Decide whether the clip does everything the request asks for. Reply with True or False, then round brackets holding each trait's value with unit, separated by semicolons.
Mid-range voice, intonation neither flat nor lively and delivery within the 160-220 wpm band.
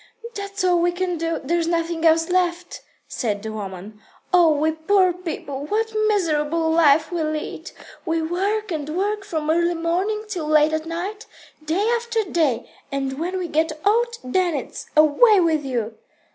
False (335 Hz; 3.3 semitones; 170 wpm)